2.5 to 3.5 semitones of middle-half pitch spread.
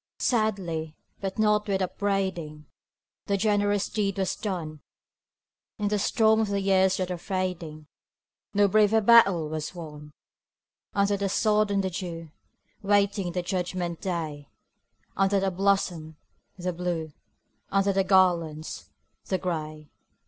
Yes: average, 3.2 semitones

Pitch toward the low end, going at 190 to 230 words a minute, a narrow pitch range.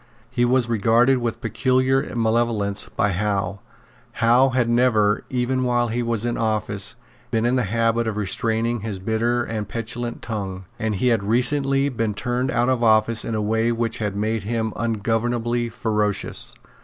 No: low, 115 Hz; average, 165 wpm; narrow, 2.1 semitones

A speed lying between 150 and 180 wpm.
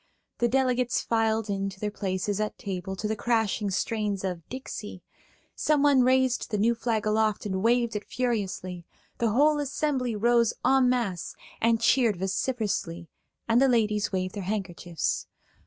Yes: average, 155 wpm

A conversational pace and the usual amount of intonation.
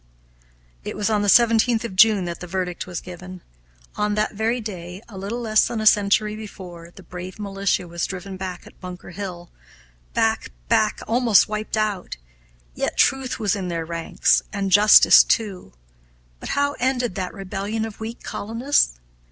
Yes: average, 170 wpm; average, 3.3 semitones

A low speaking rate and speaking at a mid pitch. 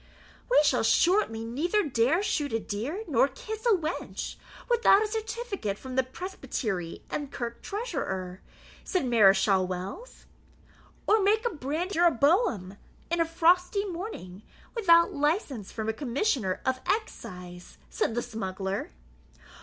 No: slow, 130 wpm; very high, 285 Hz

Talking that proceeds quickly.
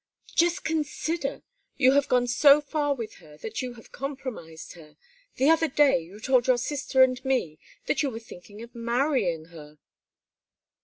No: average, 165 wpm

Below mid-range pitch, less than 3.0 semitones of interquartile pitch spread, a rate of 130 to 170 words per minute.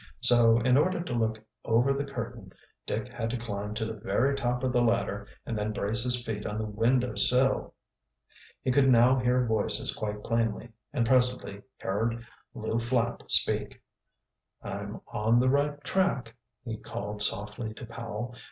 Yes: low, 115 Hz; narrow, 2.4 semitones; average, 165 wpm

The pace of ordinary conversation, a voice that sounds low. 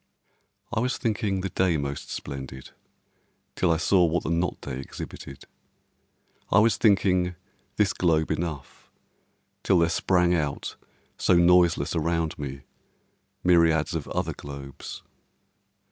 No: slow, 125 wpm; very low, 85 Hz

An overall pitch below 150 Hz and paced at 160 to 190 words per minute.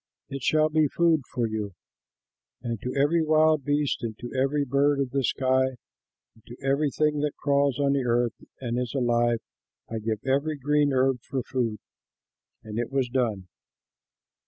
Yes: low, 135 Hz; average, 170 wpm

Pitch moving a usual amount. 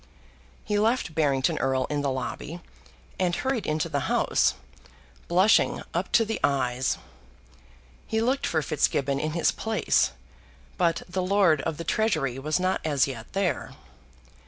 No: wide, 6.1 semitones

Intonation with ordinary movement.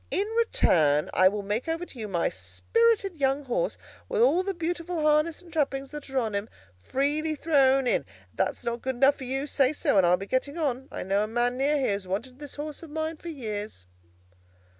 No: wide, 5.8 semitones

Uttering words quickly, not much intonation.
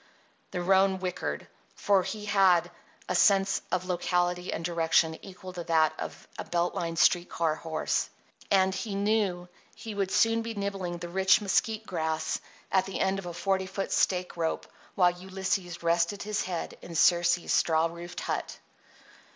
No: average, 165 wpm; narrow, 2.2 semitones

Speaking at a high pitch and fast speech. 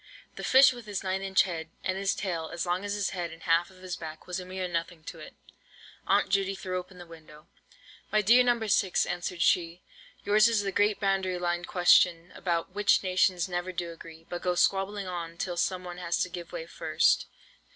No: medium, 180 Hz; fast, 215 wpm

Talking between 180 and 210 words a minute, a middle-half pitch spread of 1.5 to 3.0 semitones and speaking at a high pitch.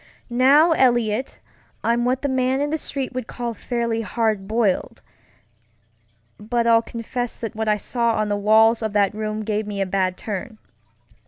No: average, 170 wpm; narrow, 2.5 semitones; high, 230 Hz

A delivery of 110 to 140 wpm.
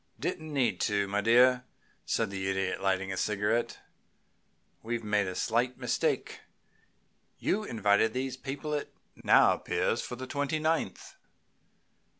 Yes: slow, 135 wpm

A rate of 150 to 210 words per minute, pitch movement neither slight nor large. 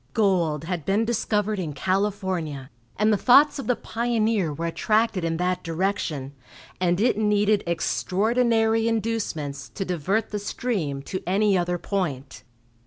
No: average, 140 wpm; average, 4.7 semitones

